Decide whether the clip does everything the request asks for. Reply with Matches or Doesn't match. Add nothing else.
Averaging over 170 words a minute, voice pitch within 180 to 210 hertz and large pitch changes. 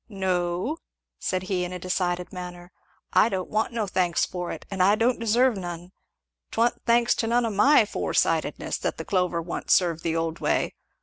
Doesn't match